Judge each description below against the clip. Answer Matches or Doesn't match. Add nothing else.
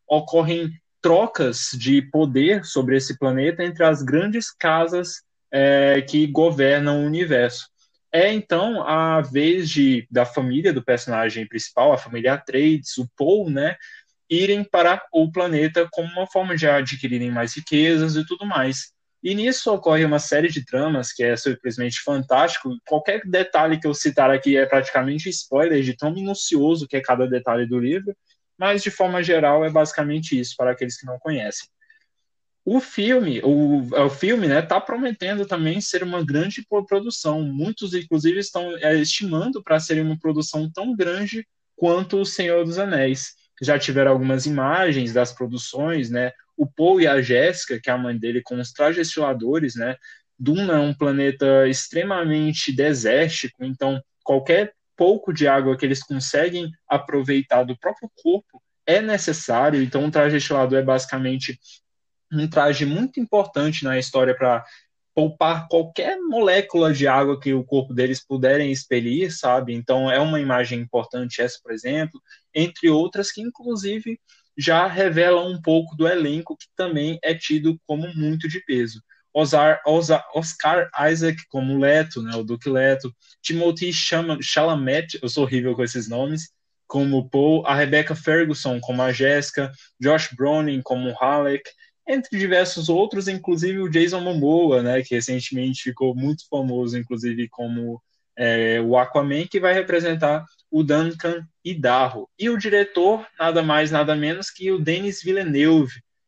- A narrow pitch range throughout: Doesn't match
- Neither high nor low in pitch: Matches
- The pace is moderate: Matches